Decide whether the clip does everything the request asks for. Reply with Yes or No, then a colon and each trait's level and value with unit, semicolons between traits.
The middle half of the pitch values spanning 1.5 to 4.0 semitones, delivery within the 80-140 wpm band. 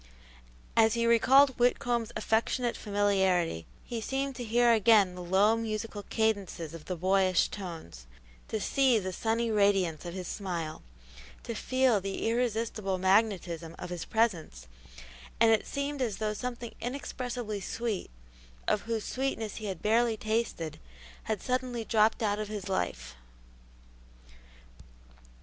Yes: average, 3.7 semitones; slow, 135 wpm